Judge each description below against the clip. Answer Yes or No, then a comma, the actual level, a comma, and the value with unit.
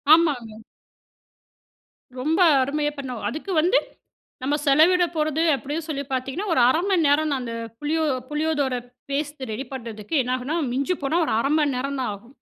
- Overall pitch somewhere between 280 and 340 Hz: Yes, very high, 285 Hz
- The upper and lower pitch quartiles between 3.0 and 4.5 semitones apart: Yes, average, 3.4 semitones